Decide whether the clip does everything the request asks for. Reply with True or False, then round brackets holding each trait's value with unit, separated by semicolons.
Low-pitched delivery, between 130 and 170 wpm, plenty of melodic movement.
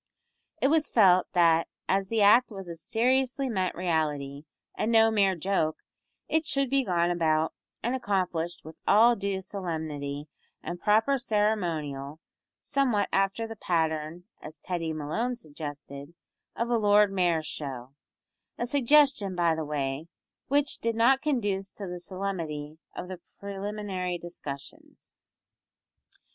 False (185 Hz; 135 wpm; 5.8 semitones)